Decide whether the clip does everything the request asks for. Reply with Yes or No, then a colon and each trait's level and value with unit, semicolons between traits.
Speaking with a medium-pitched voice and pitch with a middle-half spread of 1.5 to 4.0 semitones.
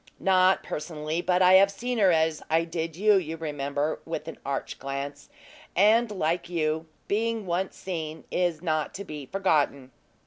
Yes: medium, 165 Hz; average, 3.5 semitones